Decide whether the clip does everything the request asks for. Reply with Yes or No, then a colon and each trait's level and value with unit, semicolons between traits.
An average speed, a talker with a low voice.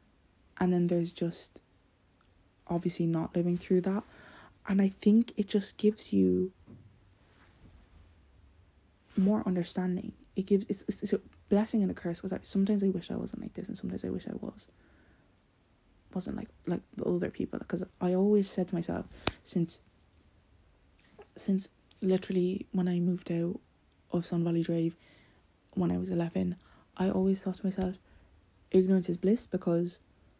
No: average, 155 wpm; medium, 175 Hz